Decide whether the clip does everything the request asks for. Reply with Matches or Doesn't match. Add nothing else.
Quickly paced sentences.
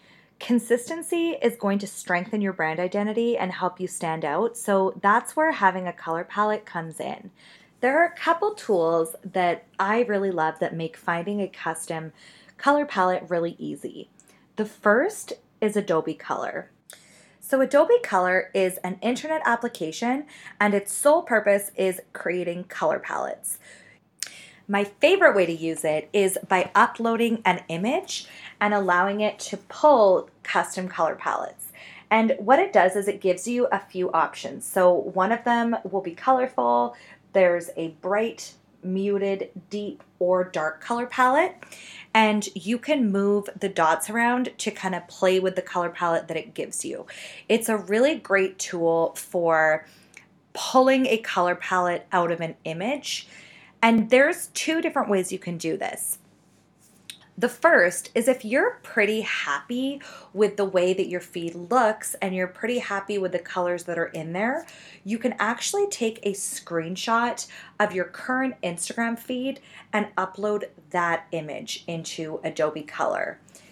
Doesn't match